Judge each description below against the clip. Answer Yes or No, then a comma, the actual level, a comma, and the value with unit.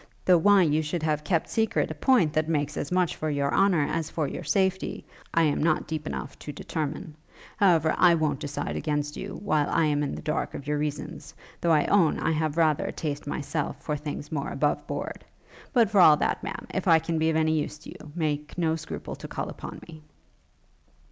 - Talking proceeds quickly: Yes, fast, 220 wpm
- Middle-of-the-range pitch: Yes, medium, 155 Hz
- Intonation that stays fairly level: Yes, narrow, 2.0 semitones